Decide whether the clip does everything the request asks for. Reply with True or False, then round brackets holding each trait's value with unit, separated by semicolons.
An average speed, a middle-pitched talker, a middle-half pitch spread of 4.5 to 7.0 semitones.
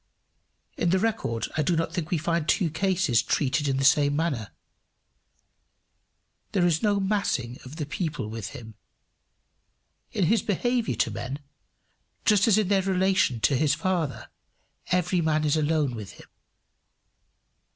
True (150 wpm; 160 Hz; 5.2 semitones)